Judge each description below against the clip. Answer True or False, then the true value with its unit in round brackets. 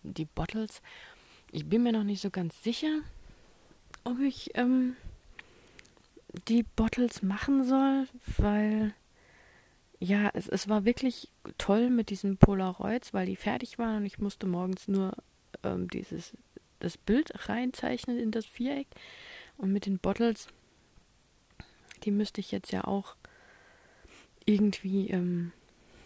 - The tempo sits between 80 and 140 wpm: True (130 wpm)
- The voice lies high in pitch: True (210 Hz)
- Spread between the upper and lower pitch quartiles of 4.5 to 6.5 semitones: False (4.0 semitones)